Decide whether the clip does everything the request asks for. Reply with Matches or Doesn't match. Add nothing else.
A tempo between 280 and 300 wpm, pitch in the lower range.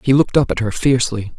Doesn't match